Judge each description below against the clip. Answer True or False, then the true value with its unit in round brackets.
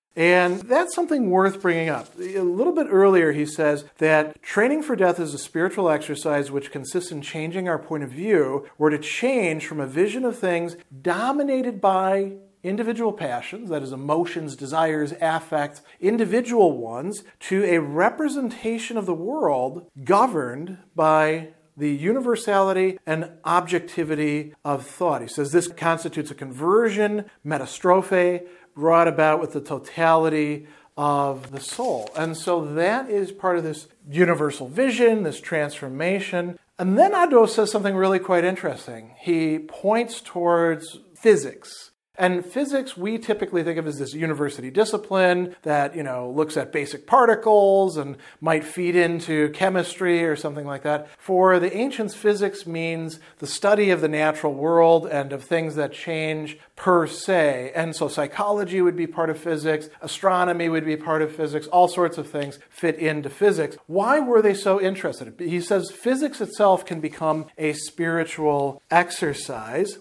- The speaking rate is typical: True (155 wpm)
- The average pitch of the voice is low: False (170 Hz)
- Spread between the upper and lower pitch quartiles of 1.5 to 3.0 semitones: False (4.1 semitones)